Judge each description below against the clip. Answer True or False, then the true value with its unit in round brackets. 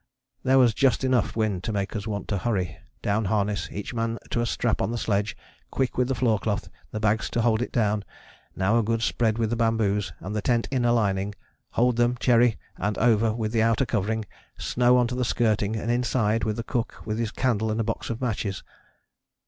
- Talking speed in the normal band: False (220 wpm)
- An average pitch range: False (2.2 semitones)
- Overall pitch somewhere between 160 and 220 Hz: False (115 Hz)